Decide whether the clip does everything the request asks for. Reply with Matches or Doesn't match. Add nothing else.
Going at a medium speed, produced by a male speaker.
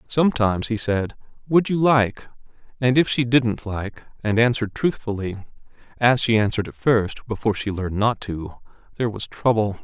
Matches